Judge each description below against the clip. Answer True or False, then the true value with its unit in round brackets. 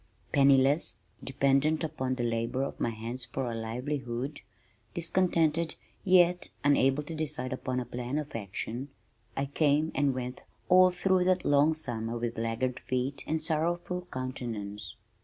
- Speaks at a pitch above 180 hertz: False (135 Hz)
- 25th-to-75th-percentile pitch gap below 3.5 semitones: False (4.4 semitones)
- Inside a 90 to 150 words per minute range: True (140 wpm)